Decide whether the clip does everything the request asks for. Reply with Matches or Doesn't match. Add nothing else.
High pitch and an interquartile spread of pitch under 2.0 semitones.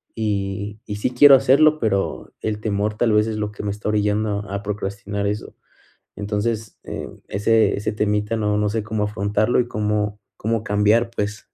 Doesn't match